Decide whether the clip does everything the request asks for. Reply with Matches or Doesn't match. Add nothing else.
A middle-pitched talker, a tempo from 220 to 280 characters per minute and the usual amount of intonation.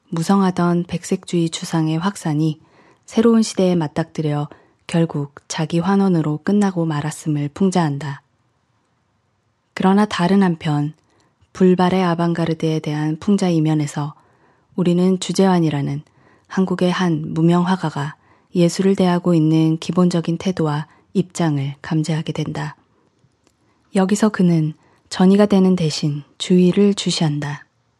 Matches